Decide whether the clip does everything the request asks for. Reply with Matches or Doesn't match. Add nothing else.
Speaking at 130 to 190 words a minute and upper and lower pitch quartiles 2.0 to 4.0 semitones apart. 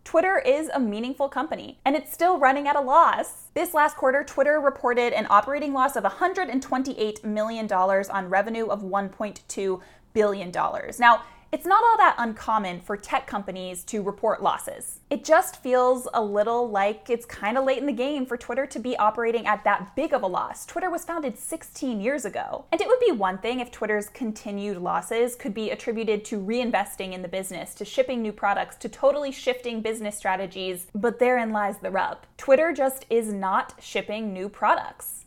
Doesn't match